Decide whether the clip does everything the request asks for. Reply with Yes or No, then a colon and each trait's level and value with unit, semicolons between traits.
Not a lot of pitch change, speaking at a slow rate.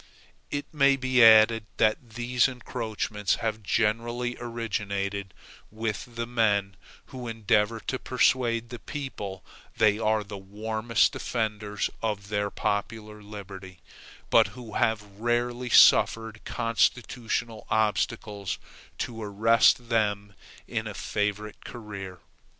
Yes: narrow, 2.3 semitones; slow, 110 wpm